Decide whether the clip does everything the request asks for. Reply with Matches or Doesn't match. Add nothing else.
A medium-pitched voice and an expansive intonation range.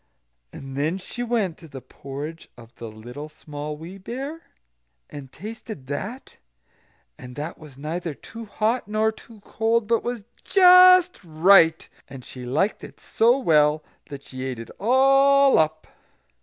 Matches